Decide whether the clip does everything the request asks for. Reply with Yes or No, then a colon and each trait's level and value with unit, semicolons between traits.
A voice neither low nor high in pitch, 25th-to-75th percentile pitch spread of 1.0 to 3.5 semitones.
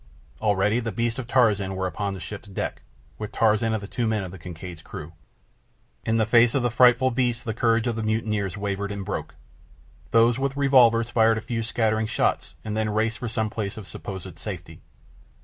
No: low, 110 Hz; narrow, 2.6 semitones